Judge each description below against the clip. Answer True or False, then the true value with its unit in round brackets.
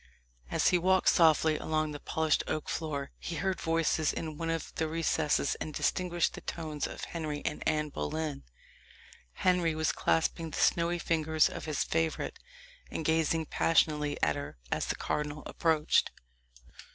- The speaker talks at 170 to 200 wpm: False (155 wpm)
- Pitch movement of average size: False (1.5 semitones)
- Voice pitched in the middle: True (160 Hz)